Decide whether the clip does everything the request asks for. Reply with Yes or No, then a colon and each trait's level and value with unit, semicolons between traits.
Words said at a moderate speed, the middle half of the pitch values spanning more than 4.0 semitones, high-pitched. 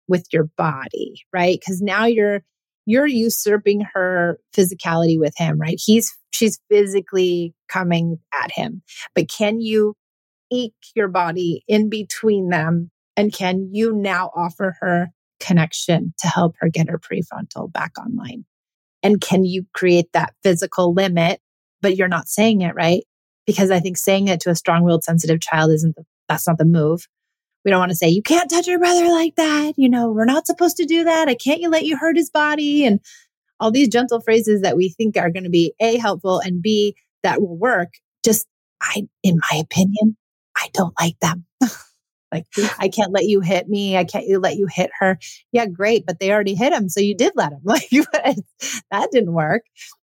Yes: average, 190 wpm; average, 4.4 semitones; high, 195 Hz